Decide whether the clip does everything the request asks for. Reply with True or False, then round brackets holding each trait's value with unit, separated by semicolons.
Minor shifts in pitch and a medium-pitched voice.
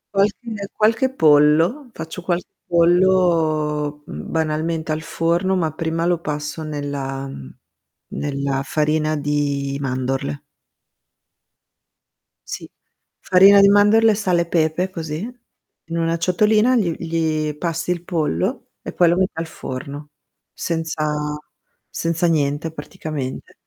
False (3.1 semitones; 160 Hz)